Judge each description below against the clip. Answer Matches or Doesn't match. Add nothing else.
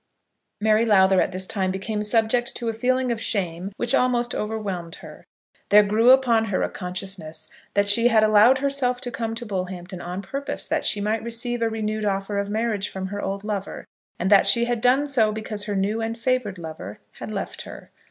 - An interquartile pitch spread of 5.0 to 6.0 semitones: Doesn't match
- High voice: Matches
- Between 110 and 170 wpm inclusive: Doesn't match